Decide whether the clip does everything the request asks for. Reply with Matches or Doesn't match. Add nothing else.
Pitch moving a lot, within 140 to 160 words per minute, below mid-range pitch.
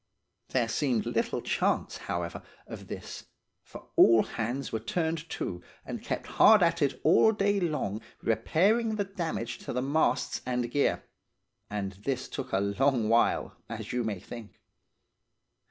Matches